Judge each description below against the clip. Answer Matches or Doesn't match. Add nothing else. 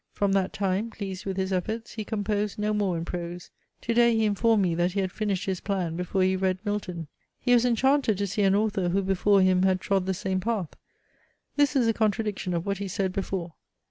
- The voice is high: Matches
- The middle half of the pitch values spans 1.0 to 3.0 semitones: Matches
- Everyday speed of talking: Doesn't match